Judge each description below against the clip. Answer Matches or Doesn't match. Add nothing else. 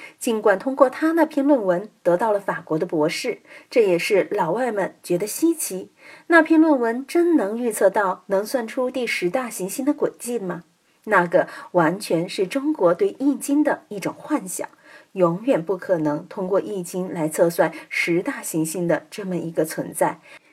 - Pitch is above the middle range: Matches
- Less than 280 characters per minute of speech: Matches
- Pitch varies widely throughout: Matches